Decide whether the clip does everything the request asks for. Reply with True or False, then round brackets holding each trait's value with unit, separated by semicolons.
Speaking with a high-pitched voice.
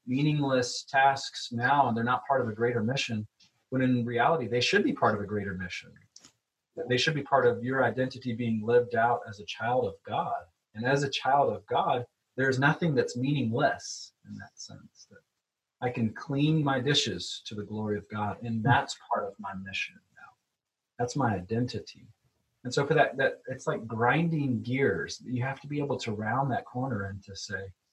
False (125 Hz)